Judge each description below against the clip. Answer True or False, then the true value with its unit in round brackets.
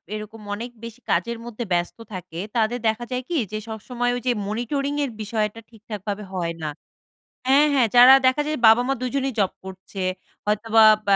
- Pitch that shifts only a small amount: False (3.0 semitones)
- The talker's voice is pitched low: False (225 Hz)